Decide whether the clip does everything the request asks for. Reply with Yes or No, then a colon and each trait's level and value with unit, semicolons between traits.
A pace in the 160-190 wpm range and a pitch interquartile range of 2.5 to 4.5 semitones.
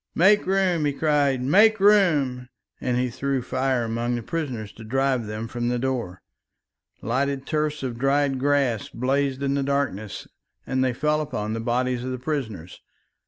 Yes: average, 165 wpm; average, 3.1 semitones